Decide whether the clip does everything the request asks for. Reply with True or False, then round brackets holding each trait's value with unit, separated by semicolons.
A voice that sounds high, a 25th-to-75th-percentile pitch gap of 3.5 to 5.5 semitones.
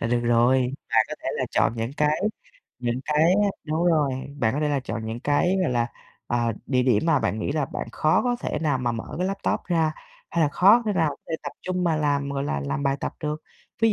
False (145 Hz; 5.0 semitones)